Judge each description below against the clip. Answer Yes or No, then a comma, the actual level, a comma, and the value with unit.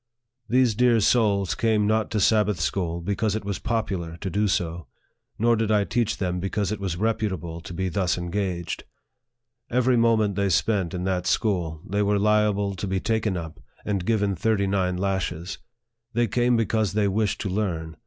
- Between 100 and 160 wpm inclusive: No, average, 180 wpm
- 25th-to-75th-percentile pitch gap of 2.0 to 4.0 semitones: Yes, average, 3.3 semitones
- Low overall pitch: Yes, low, 100 Hz